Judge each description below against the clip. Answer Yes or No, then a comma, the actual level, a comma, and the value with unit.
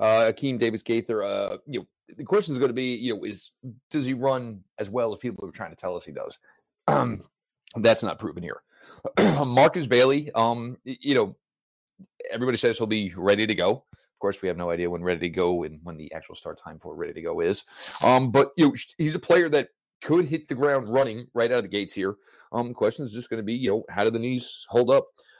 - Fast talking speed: Yes, fast, 245 wpm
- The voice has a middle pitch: No, low, 125 Hz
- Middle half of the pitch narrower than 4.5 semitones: No, average, 4.8 semitones